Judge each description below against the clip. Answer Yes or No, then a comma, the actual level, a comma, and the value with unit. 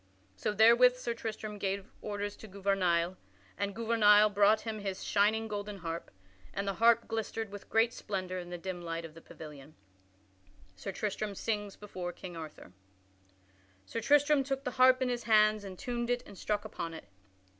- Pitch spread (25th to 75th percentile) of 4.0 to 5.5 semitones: No, average, 3.2 semitones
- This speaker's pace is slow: No, average, 175 wpm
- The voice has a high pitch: Yes, high, 205 Hz